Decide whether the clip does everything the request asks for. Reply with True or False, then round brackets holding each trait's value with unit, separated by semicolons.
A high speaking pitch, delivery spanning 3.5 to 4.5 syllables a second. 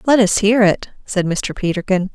False (200 Hz; 4.7 syllables/s)